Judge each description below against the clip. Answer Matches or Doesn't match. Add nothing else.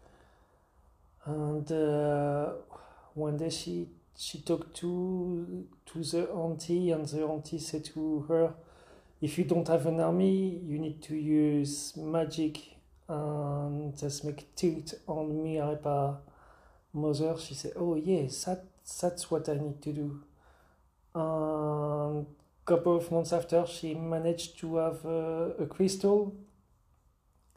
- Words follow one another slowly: Matches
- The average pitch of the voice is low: Doesn't match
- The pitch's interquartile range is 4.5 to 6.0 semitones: Doesn't match